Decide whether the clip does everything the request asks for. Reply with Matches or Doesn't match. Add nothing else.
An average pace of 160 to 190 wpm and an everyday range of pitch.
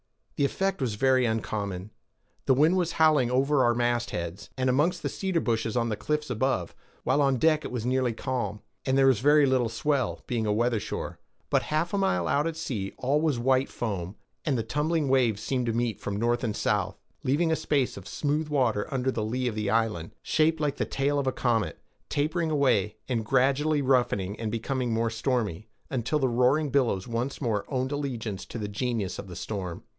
Doesn't match